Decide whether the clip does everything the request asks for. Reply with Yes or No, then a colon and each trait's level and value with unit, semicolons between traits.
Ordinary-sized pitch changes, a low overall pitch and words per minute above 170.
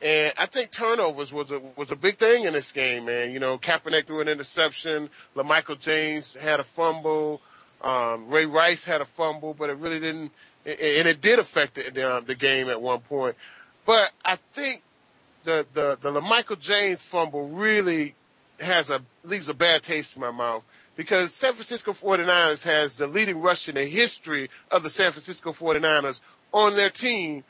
No: average, 4.2 semitones; medium, 155 Hz; average, 180 wpm